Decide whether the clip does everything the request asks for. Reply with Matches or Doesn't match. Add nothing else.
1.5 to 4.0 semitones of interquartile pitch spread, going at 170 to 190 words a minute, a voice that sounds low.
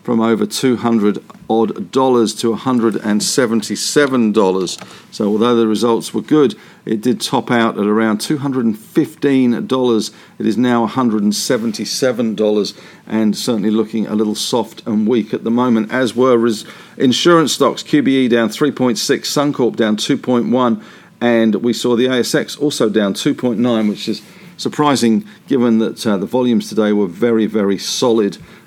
Matches